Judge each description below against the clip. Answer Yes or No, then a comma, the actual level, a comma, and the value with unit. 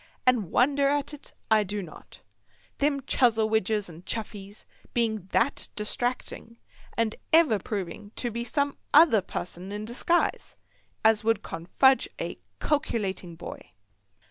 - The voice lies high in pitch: Yes, high, 220 Hz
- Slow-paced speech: Yes, slow, 125 wpm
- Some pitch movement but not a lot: Yes, average, 4.5 semitones